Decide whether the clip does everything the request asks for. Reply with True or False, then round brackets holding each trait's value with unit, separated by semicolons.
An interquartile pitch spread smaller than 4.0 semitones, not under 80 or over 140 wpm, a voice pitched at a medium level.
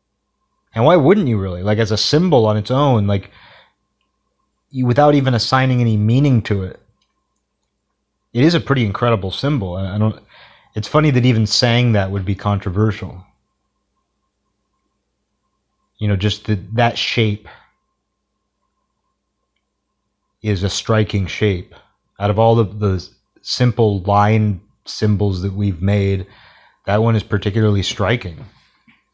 False (2.9 semitones; 135 wpm; 105 Hz)